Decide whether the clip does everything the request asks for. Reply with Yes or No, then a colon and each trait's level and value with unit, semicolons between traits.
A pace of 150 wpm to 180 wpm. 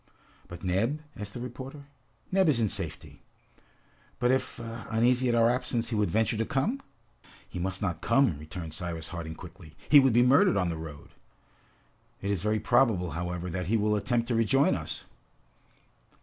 Yes: average, 175 wpm